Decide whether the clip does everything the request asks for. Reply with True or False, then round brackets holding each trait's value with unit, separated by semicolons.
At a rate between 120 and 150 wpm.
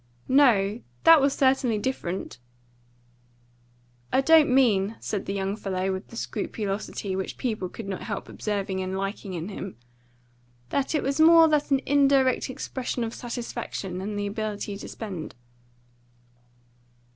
True (140 wpm)